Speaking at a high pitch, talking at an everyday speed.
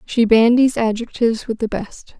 Yes: high, 230 Hz; average, 165 wpm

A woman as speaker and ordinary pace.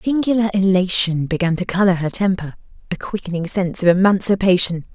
Yes: female; average, 160 wpm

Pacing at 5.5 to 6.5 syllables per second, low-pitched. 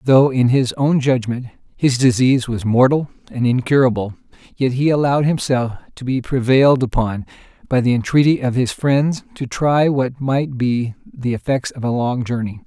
No: 4.9 syllables/s; low, 130 Hz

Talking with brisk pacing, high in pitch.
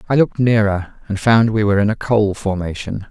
No: fast, 215 wpm; low, 105 Hz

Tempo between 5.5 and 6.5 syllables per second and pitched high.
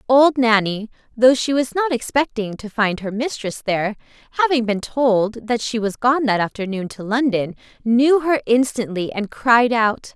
No: 4.5 syllables/s; high, 235 Hz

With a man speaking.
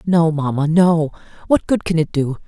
No: female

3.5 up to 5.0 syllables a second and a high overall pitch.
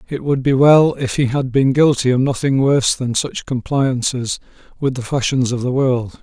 No: 4.8 syllables/s; low, 130 Hz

